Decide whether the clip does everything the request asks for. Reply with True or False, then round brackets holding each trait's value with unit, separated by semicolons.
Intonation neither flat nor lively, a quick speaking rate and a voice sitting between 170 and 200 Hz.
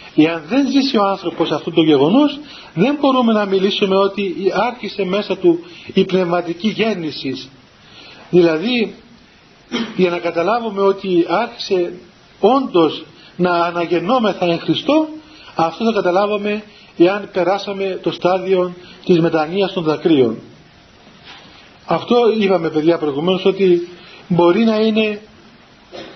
False (3.7 semitones; 110 wpm; 190 Hz)